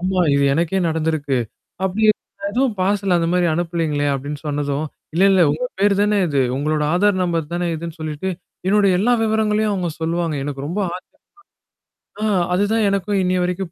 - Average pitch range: Yes, average, 4.1 semitones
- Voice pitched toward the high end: No, medium, 175 Hz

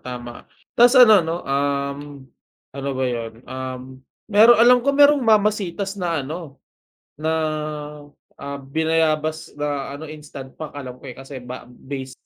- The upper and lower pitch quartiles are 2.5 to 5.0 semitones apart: No, wide, 5.6 semitones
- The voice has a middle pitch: Yes, medium, 145 Hz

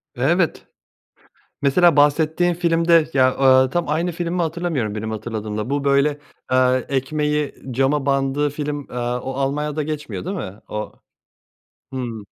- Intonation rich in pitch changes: No, average, 3.6 semitones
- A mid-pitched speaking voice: Yes, medium, 145 Hz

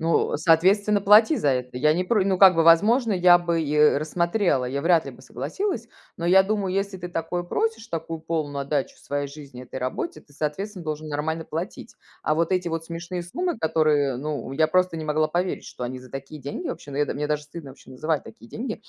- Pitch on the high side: No, medium, 165 Hz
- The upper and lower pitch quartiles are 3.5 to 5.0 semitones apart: Yes, average, 3.8 semitones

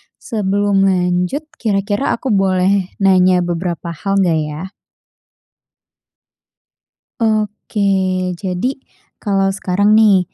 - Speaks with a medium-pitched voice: No, high, 195 Hz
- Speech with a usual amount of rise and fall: No, narrow, 2.1 semitones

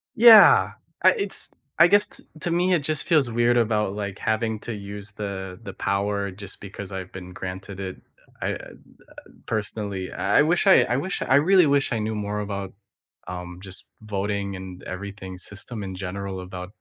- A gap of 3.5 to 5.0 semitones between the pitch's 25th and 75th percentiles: Yes, average, 3.8 semitones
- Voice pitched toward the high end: No, low, 100 Hz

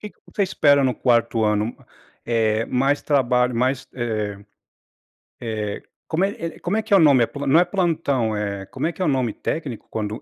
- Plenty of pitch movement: Yes, wide, 6.1 semitones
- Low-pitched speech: Yes, low, 130 Hz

